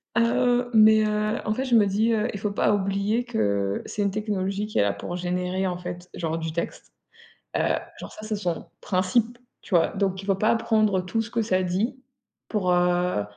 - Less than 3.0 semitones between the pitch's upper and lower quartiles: No, average, 3.3 semitones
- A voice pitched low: No, high, 200 Hz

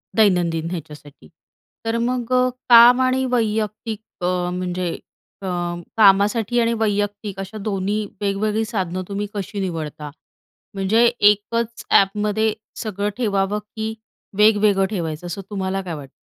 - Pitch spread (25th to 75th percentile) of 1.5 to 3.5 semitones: Yes, average, 2.9 semitones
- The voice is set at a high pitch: Yes, high, 205 Hz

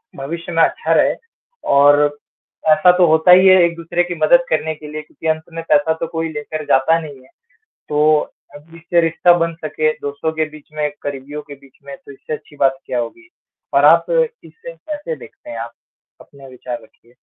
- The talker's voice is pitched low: No, medium, 155 Hz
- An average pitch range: Yes, average, 3.0 semitones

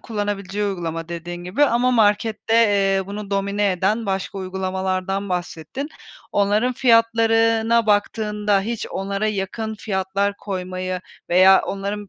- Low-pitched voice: No, high, 200 Hz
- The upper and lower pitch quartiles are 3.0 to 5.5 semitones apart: No, narrow, 2.5 semitones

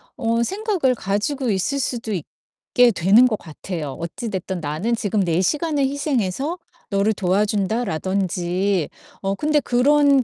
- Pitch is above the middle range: Yes, high, 215 Hz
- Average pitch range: No, wide, 6.1 semitones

